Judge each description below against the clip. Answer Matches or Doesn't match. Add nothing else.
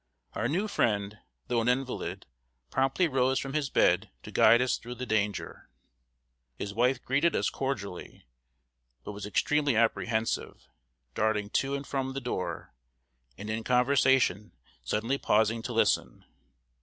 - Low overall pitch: Matches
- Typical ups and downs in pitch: Matches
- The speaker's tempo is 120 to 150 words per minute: Matches